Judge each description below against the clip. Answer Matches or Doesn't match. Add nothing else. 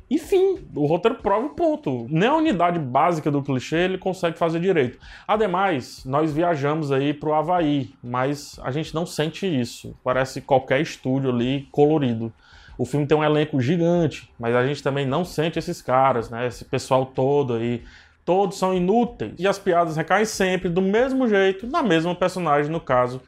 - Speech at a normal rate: Matches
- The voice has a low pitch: Doesn't match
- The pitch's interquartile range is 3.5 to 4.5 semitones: Doesn't match